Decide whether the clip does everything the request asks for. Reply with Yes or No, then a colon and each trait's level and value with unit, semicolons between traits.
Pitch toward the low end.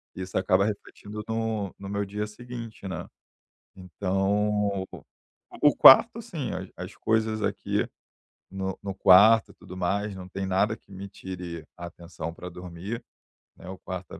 Yes: low, 100 Hz